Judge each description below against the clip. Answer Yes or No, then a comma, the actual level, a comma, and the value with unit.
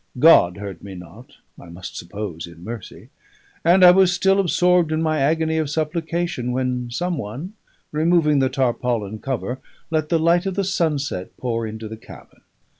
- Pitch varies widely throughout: Yes, wide, 7.3 semitones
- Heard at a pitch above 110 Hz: Yes, medium, 140 Hz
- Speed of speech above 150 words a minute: Yes, average, 170 wpm